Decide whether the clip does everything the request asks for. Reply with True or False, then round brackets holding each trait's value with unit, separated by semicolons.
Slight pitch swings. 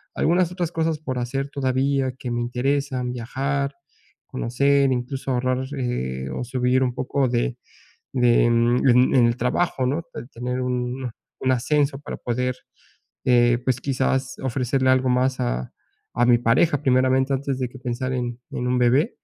True (1.8 semitones)